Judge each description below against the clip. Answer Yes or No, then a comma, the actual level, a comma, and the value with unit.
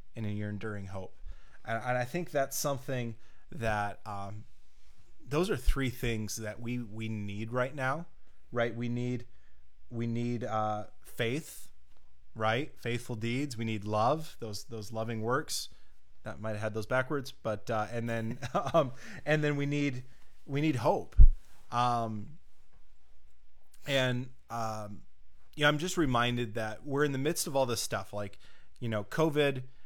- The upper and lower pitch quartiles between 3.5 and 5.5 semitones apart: Yes, average, 3.8 semitones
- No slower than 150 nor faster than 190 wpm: Yes, average, 160 wpm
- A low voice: Yes, low, 115 Hz